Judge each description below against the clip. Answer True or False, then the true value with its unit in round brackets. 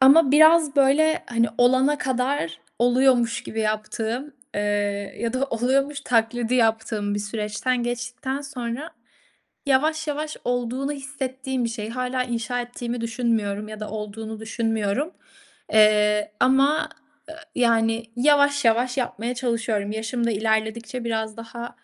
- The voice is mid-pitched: False (240 Hz)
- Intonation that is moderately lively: True (3.1 semitones)